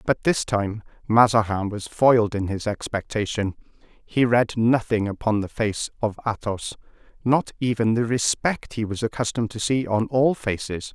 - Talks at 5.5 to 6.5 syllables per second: No, 4.7 syllables/s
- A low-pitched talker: Yes, low, 110 Hz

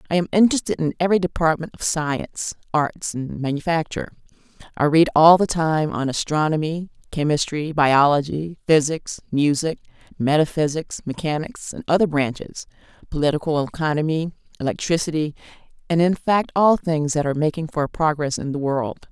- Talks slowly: Yes, slow, 130 wpm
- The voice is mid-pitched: Yes, medium, 155 Hz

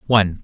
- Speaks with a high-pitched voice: No, low, 100 Hz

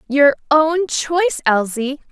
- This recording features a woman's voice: Yes, female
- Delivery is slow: Yes, slow, 115 wpm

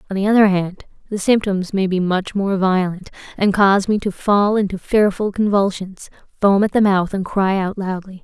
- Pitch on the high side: Yes, high, 195 Hz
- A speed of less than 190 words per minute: No, average, 195 wpm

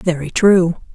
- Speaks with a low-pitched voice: No, medium, 175 Hz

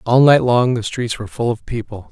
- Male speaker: Yes, male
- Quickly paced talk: Yes, fast, 255 wpm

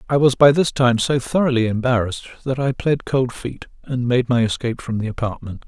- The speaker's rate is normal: No, fast, 210 wpm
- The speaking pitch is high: No, low, 125 Hz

